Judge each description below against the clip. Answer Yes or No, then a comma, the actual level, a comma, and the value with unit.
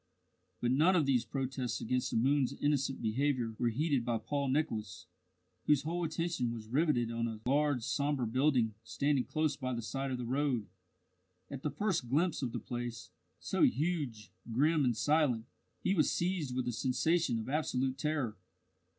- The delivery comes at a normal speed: Yes, average, 170 wpm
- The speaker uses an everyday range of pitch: Yes, average, 3.9 semitones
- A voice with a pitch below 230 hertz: Yes, low, 135 Hz